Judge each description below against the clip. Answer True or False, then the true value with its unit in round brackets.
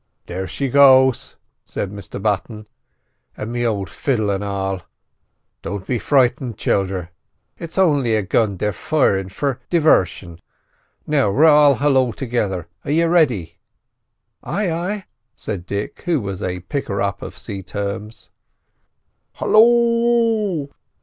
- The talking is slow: True (125 wpm)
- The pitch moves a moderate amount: False (7.1 semitones)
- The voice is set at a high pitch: False (115 Hz)